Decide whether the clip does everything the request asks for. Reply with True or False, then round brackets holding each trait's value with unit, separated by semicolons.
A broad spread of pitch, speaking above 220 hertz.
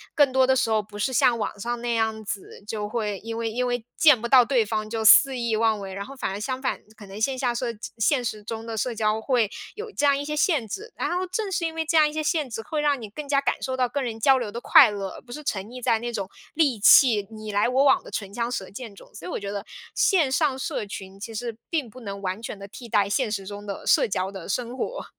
False (4.2 semitones; 235 Hz)